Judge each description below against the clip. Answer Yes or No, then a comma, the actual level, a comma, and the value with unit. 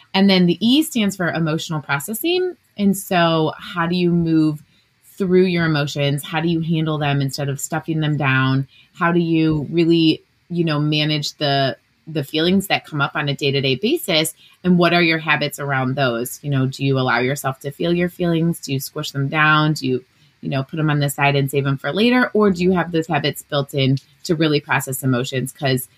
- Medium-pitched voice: Yes, medium, 150 Hz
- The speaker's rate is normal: No, fast, 215 wpm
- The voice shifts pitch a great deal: No, average, 3.5 semitones